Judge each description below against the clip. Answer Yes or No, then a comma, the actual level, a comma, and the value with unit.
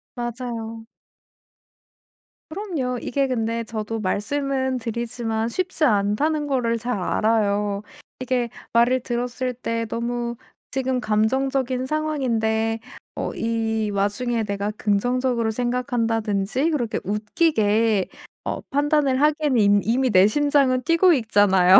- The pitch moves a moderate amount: Yes, average, 3.1 semitones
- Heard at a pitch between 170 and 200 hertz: No, high, 235 Hz